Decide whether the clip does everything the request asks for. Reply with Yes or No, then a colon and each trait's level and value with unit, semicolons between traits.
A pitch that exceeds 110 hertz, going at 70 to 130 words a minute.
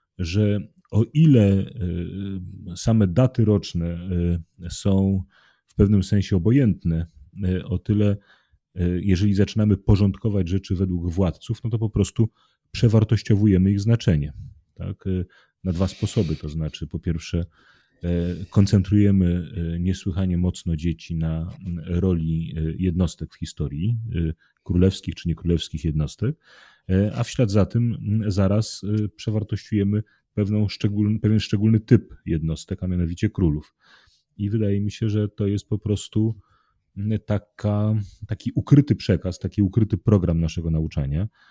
No: low, 100 Hz; average, 120 wpm